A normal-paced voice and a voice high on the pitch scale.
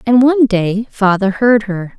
Yes: average, 180 wpm; high, 215 Hz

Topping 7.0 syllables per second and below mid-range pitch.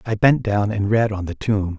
No: 4.8 syllables/s; low, 105 Hz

